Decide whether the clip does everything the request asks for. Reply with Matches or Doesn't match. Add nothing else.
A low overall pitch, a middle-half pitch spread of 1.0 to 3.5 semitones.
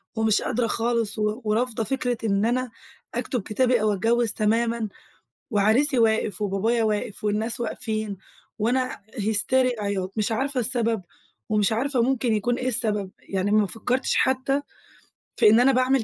Doesn't match